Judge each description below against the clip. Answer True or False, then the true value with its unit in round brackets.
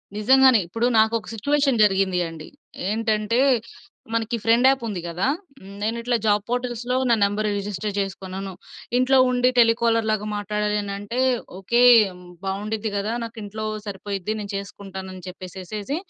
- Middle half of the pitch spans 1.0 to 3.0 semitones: True (2.7 semitones)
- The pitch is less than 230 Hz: True (215 Hz)